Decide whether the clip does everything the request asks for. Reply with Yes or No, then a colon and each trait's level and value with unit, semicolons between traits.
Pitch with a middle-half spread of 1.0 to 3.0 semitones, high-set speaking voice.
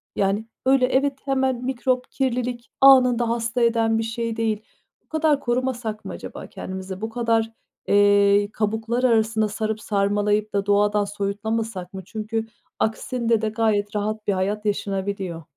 Yes: average, 2.7 semitones; high, 220 Hz